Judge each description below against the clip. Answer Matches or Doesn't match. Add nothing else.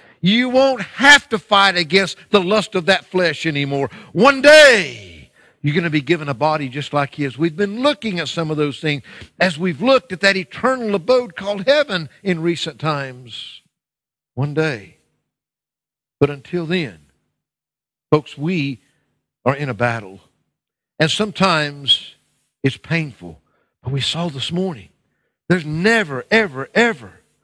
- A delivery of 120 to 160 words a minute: Matches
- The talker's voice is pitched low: Doesn't match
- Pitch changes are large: Matches